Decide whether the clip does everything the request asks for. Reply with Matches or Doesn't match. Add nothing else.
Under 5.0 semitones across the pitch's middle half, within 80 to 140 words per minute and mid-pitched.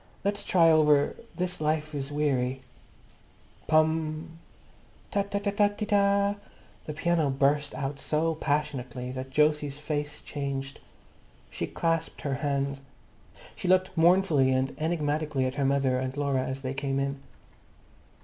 Matches